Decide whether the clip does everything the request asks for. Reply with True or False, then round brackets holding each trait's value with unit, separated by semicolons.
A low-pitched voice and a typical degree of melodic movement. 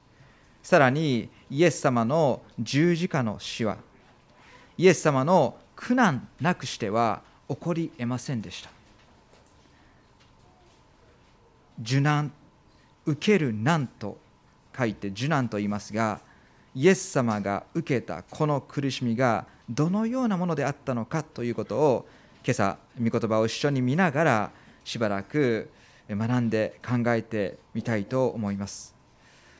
False (125 Hz; 5.7 semitones)